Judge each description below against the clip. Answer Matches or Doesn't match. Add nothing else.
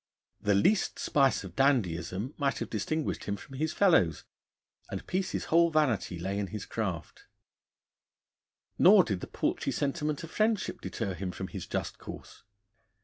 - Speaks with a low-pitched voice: Matches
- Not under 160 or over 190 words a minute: Doesn't match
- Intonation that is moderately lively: Doesn't match